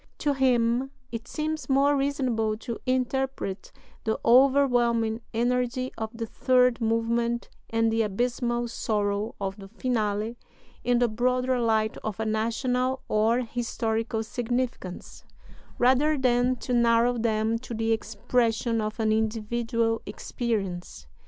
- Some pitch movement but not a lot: No, narrow, 2.1 semitones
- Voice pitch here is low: No, high, 235 Hz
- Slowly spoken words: Yes, slow, 125 wpm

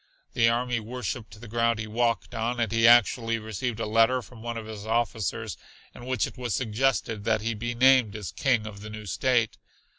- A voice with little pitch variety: Yes, narrow, 1.8 semitones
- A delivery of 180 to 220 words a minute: Yes, fast, 205 wpm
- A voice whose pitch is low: Yes, low, 115 Hz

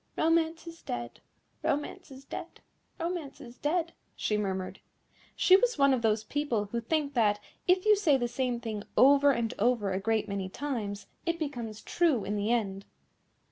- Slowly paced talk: No, average, 175 wpm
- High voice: Yes, very high, 250 Hz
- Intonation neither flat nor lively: No, wide, 6.9 semitones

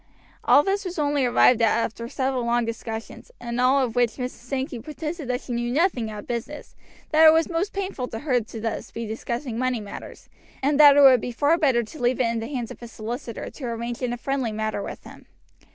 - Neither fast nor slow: No, fast, 230 wpm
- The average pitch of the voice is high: Yes, high, 245 Hz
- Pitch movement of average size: Yes, average, 3.7 semitones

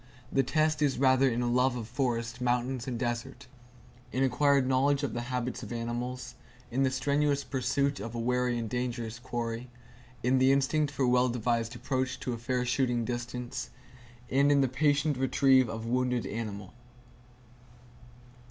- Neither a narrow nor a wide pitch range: No, narrow, 2.1 semitones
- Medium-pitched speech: No, low, 125 Hz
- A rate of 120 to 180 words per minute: Yes, average, 170 wpm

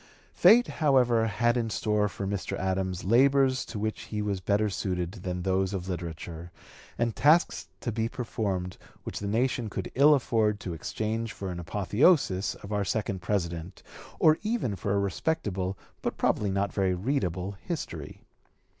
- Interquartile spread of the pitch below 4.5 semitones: Yes, average, 4.1 semitones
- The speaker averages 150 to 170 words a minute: Yes, average, 160 wpm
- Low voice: Yes, low, 105 Hz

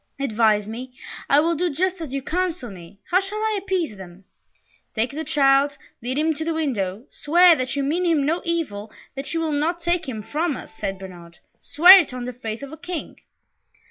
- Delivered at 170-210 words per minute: Yes, fast, 205 wpm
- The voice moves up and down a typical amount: No, wide, 6.8 semitones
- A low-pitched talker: No, very high, 285 Hz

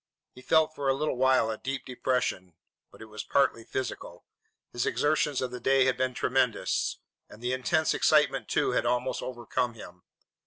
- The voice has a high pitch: No, low, 130 Hz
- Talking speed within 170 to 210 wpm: Yes, average, 180 wpm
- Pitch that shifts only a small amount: Yes, narrow, 1.8 semitones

